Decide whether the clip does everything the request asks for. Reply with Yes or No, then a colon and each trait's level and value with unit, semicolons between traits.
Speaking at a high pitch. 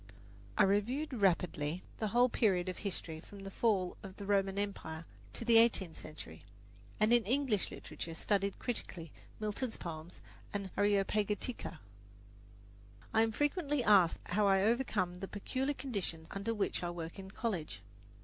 Yes: high, 200 Hz